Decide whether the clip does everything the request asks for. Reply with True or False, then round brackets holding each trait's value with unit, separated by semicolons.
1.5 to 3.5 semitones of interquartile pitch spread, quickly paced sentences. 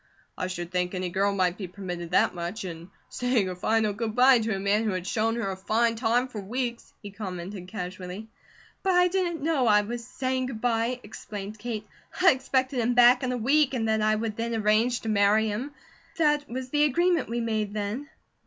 False (4.0 semitones; 210 wpm)